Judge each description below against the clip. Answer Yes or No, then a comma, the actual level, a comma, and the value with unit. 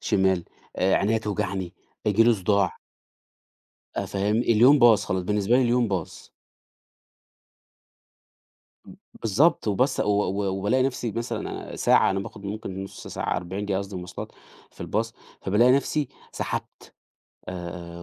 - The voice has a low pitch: Yes, low, 105 Hz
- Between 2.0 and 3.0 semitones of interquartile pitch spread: No, average, 3.5 semitones